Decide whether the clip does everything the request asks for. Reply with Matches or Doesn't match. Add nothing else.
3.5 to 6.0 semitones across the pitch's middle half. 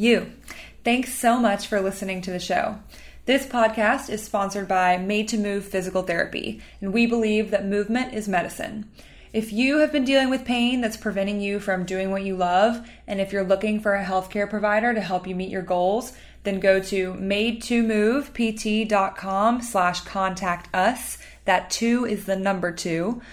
Doesn't match